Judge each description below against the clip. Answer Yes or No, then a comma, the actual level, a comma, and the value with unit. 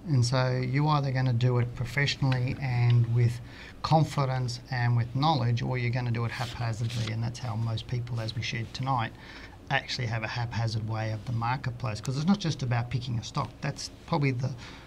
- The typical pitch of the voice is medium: No, low, 125 Hz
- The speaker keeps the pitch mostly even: Yes, narrow, 2.2 semitones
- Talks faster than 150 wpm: Yes, average, 200 wpm